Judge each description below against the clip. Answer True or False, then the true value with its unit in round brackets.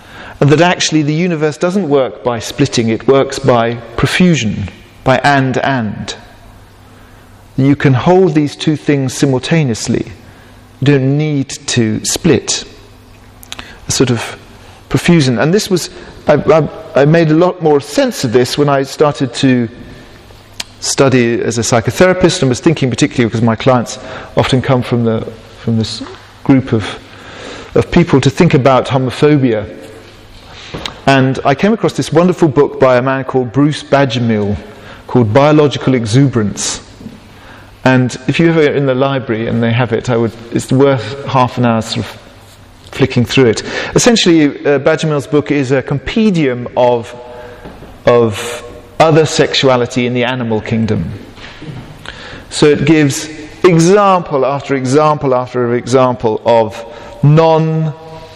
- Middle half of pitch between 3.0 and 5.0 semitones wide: True (4.1 semitones)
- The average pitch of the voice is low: True (130 Hz)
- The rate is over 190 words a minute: False (140 wpm)